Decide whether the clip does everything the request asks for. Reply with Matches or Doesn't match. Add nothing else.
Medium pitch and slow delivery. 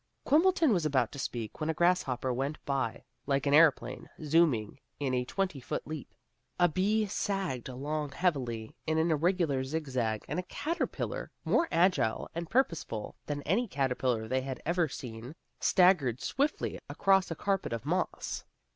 Doesn't match